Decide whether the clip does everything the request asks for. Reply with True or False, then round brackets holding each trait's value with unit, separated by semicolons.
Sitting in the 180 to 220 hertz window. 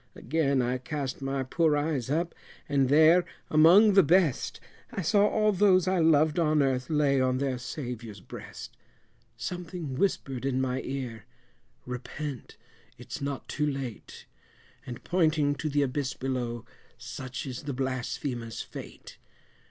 False (140 Hz)